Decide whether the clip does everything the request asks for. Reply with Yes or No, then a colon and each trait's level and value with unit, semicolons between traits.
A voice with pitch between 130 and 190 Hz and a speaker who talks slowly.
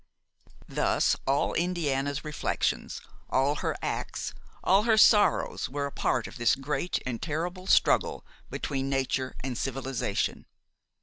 Yes: medium, 140 Hz; slow, 125 wpm